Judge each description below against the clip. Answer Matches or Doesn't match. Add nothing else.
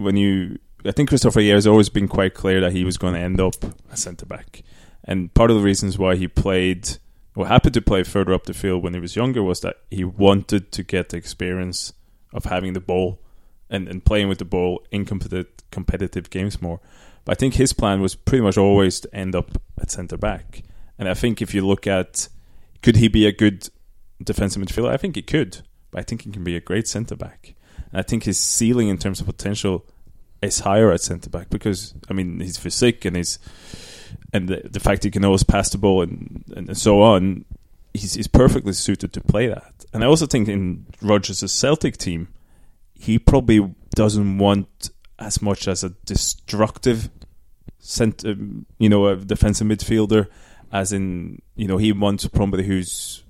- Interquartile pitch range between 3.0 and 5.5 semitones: Doesn't match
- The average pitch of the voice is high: Doesn't match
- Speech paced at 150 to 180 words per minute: Doesn't match